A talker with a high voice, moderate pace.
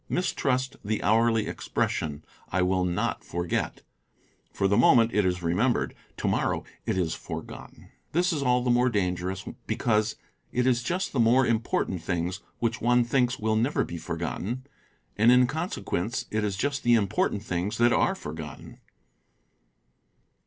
No: low, 110 Hz; average, 150 wpm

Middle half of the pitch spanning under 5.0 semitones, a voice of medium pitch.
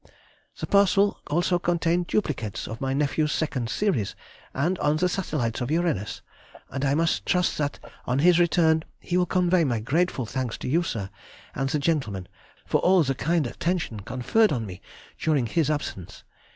No: wide, 5.6 semitones; medium, 155 Hz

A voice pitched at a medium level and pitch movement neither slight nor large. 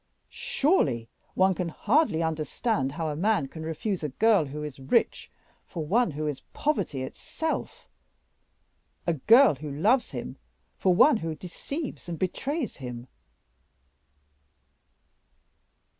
No: medium, 165 Hz; wide, 7.0 semitones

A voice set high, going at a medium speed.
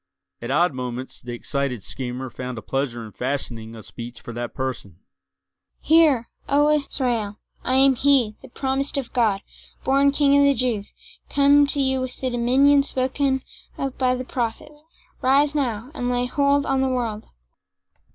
Yes: very high, 255 Hz; average, 160 wpm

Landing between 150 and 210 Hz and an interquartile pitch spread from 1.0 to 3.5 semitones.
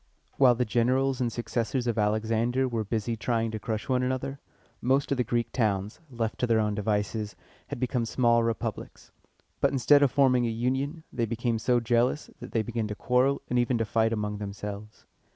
No: low, 115 Hz; narrow, 2.4 semitones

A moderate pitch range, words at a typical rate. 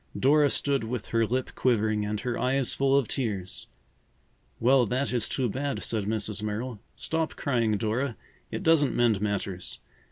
Yes: average, 4.1 semitones; average, 160 wpm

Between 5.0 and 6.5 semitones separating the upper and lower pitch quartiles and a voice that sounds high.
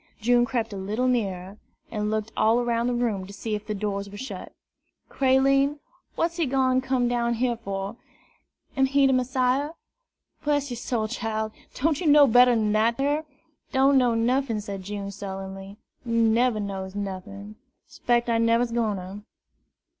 No: average, 3.8 semitones; high, 230 Hz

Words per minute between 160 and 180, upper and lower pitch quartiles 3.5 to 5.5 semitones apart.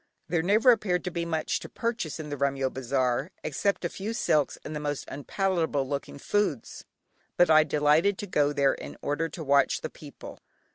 No: average, 190 wpm; average, 4.2 semitones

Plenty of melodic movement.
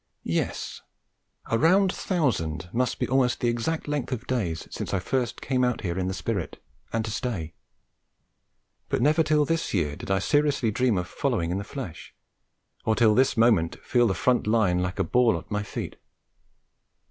Yes: wide, 5.7 semitones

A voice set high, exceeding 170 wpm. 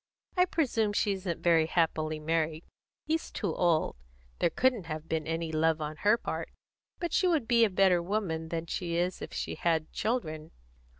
No: medium, 170 Hz; average, 180 wpm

